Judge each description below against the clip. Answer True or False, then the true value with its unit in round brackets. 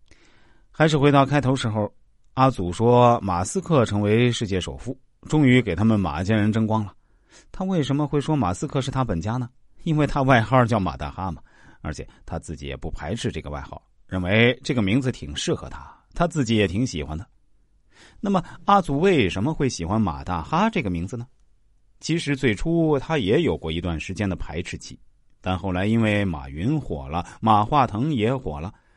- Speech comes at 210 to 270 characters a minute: False (280 characters per minute)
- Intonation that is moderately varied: False (6.7 semitones)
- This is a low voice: True (110 Hz)